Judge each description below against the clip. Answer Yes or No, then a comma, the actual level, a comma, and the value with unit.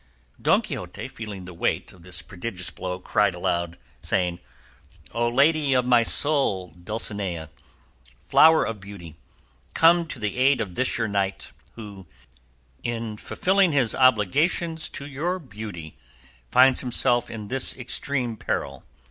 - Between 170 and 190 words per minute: No, slow, 135 wpm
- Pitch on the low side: Yes, low, 115 Hz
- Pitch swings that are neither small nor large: No, wide, 6.0 semitones